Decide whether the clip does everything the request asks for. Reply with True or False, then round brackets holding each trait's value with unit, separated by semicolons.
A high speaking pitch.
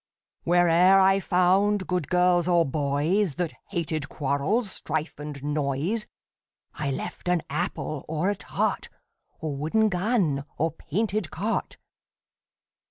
False (175 Hz)